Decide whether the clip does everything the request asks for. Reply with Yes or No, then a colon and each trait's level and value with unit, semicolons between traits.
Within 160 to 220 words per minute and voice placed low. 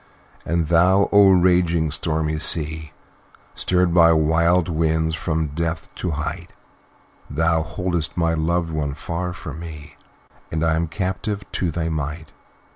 No: slow, 135 wpm; very low, 80 Hz